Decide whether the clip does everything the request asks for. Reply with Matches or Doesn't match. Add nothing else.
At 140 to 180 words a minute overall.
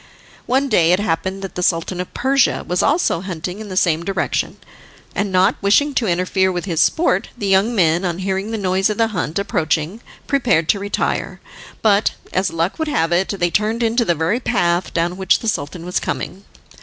Doesn't match